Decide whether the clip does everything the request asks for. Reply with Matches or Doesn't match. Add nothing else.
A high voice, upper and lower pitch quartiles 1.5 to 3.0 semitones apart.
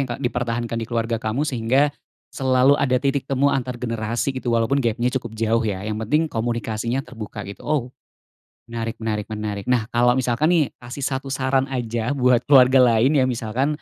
Doesn't match